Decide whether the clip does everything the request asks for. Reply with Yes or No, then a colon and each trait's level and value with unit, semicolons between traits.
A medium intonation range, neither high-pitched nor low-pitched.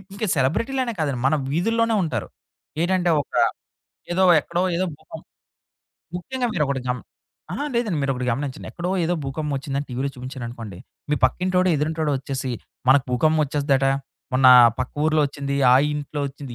Yes: average, 4.8 semitones; medium, 145 Hz